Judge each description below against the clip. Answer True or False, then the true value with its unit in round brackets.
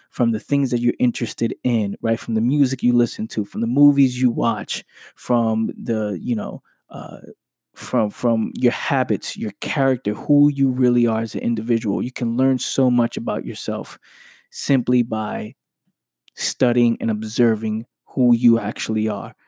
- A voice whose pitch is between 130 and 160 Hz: False (120 Hz)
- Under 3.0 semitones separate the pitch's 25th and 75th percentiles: True (2.5 semitones)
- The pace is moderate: True (165 wpm)